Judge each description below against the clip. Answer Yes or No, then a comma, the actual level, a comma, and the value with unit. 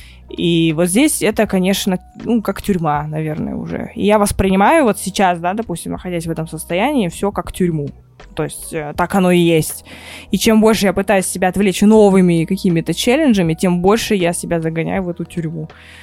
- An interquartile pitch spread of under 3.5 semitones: No, average, 3.8 semitones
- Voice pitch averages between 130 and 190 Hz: Yes, medium, 185 Hz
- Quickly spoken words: Yes, fast, 180 wpm